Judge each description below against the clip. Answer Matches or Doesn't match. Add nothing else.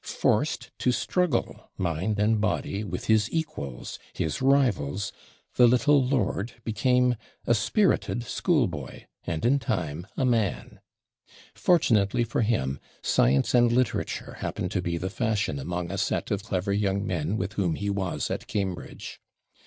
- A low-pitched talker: Matches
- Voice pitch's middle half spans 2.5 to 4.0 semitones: Doesn't match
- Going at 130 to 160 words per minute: Matches